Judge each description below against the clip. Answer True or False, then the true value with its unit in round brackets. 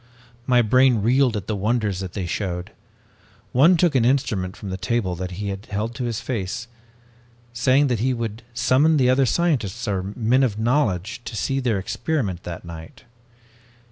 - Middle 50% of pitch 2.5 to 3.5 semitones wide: False (4.7 semitones)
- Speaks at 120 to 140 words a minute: False (170 wpm)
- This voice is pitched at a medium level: False (115 Hz)